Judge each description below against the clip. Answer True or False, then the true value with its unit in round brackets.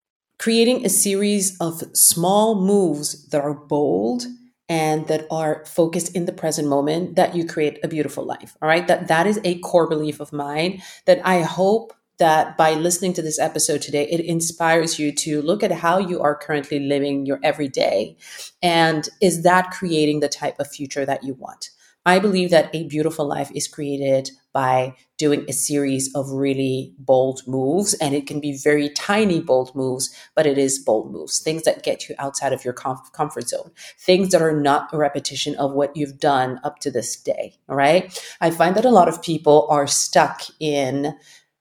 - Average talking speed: True (190 wpm)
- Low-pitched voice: False (155 Hz)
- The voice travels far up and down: False (3.4 semitones)